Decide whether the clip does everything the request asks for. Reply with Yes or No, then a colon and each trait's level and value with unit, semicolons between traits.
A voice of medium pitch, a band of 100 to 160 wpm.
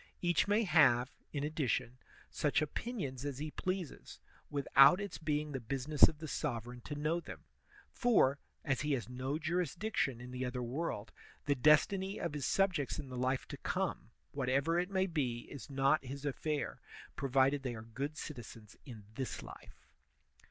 No: medium, 145 Hz; average, 170 wpm